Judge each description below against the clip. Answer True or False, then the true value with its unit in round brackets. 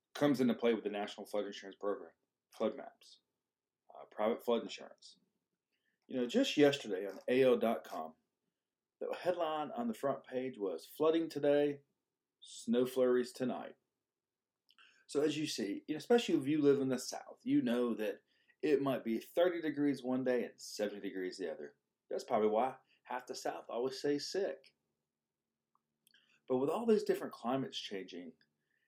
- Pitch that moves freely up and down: True (6.7 semitones)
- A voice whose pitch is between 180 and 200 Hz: False (135 Hz)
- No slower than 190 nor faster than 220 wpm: False (155 wpm)